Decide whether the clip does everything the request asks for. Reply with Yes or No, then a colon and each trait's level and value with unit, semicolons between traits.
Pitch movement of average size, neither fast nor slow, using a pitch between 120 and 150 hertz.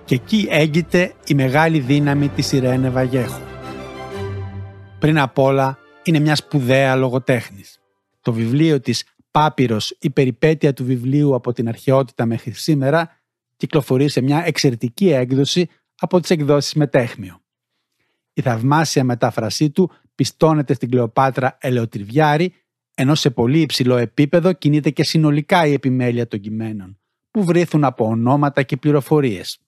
Yes: average, 4.0 semitones; average, 130 wpm; low, 135 Hz